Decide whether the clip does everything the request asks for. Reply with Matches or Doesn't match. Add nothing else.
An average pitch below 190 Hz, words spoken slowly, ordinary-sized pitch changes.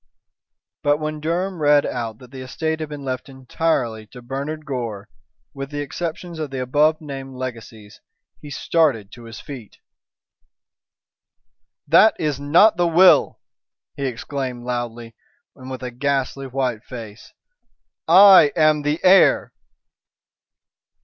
Matches